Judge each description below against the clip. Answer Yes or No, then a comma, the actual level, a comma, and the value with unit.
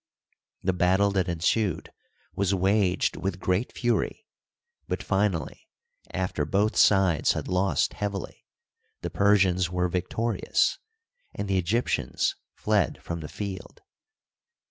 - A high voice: No, very low, 95 Hz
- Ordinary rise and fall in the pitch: No, narrow, 2.1 semitones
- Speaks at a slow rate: Yes, slow, 120 wpm